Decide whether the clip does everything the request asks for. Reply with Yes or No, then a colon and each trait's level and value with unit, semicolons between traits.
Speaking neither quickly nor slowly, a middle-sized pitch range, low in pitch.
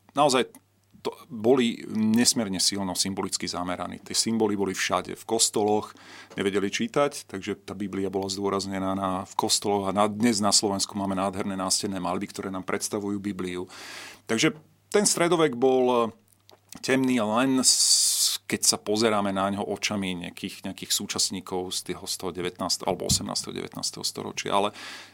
Yes: average, 145 wpm; average, 3.0 semitones; low, 100 Hz